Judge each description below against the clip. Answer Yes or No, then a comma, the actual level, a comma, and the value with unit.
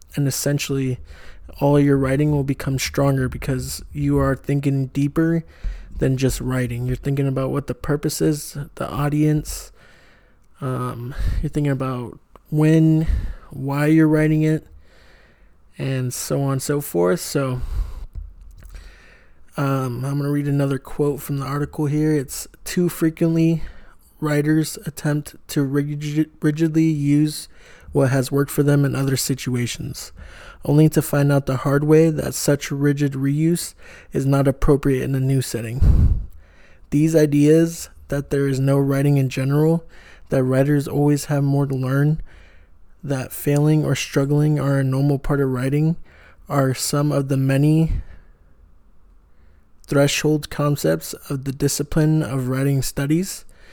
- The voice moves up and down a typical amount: No, narrow, 2.3 semitones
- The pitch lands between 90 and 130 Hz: No, medium, 140 Hz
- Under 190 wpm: Yes, average, 140 wpm